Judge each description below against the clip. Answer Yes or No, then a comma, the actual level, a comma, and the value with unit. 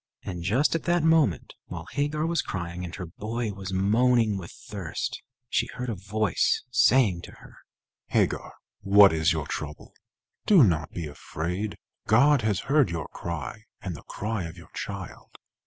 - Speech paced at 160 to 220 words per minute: Yes, average, 165 wpm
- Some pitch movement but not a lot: No, wide, 6.4 semitones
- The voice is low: Yes, low, 100 Hz